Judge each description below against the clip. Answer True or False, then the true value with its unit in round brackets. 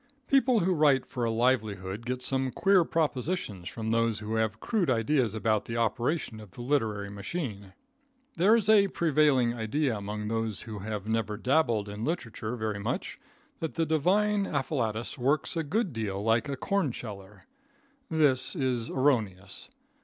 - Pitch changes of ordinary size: False (5.9 semitones)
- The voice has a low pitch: True (120 Hz)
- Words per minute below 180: True (160 wpm)